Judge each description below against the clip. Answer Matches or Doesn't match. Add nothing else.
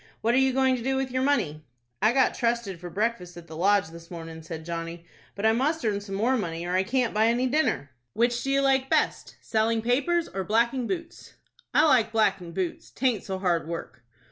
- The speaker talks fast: Matches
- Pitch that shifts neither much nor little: Doesn't match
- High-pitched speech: Matches